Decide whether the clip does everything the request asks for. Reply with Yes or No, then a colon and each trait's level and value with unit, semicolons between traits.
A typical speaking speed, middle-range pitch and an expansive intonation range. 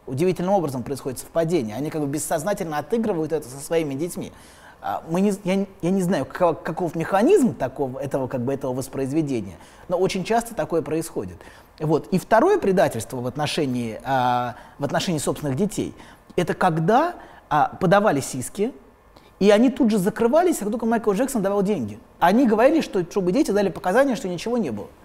No: fast, 165 wpm; medium, 175 Hz; wide, 6.5 semitones